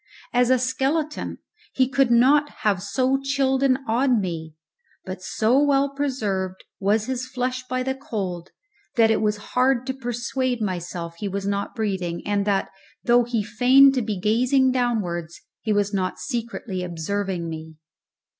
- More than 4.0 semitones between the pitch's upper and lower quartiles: Yes, average, 4.9 semitones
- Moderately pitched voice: No, high, 230 Hz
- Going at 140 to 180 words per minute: Yes, average, 155 wpm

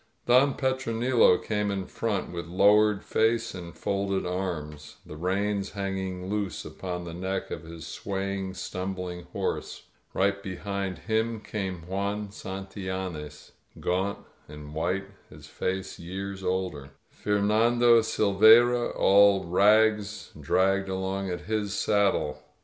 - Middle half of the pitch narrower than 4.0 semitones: Yes, narrow, 2.4 semitones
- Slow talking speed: Yes, slow, 120 wpm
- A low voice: Yes, very low, 95 Hz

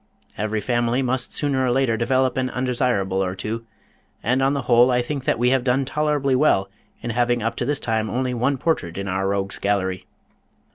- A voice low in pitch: Yes, low, 120 Hz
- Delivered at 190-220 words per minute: Yes, average, 200 wpm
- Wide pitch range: No, average, 3.5 semitones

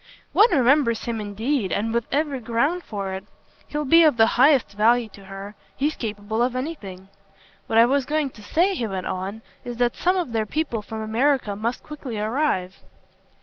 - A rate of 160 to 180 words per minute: No, average, 190 wpm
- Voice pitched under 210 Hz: No, high, 235 Hz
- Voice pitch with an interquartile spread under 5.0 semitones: No, average, 5.3 semitones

